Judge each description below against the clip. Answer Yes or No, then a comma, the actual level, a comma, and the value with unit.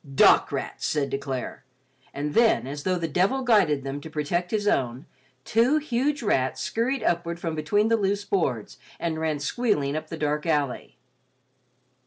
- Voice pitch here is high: No, medium, 165 Hz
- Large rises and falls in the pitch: Yes, wide, 6.6 semitones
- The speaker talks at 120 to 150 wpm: No, average, 170 wpm